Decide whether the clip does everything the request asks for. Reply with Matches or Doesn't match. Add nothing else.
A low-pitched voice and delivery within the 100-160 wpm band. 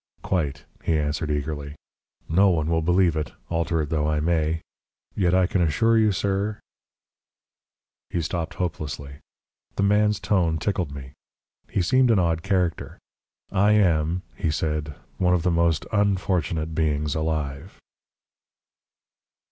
Matches